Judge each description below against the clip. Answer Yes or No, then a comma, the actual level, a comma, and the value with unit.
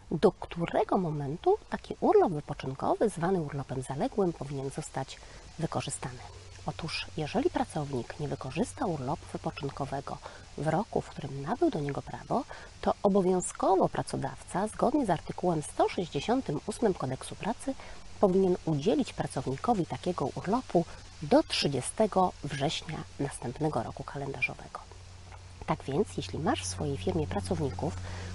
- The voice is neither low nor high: Yes, medium, 150 Hz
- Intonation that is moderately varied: No, wide, 6.3 semitones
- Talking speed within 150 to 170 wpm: No, average, 115 wpm